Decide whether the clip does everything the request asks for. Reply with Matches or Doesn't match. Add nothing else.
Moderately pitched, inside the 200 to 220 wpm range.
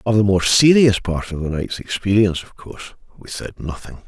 Doesn't match